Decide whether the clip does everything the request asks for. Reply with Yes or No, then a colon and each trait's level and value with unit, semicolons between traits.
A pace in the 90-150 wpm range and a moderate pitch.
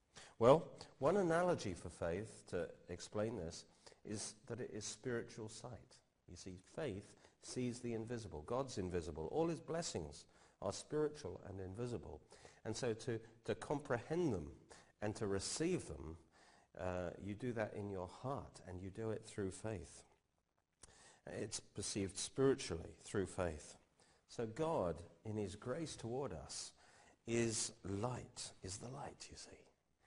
No: average, 140 wpm; low, 105 Hz